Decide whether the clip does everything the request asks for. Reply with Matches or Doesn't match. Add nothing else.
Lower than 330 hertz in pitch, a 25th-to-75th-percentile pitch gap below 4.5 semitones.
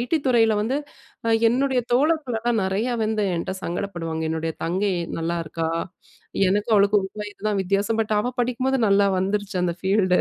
Matches